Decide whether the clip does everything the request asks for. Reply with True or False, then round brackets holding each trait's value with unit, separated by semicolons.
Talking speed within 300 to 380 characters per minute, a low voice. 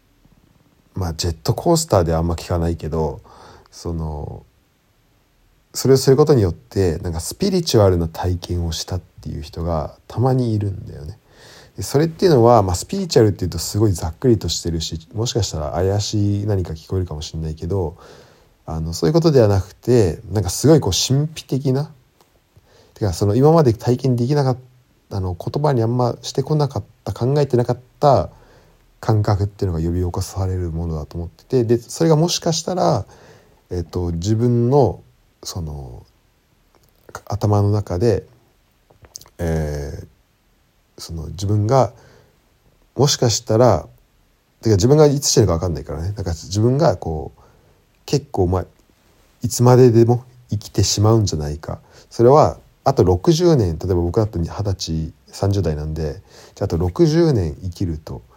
True (305 characters per minute; 105 Hz)